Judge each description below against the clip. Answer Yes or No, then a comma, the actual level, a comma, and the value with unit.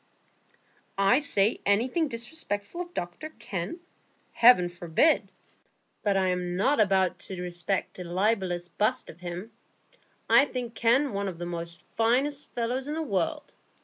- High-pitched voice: Yes, high, 205 Hz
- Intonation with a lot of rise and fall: Yes, wide, 6.2 semitones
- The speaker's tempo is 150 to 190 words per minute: No, average, 140 wpm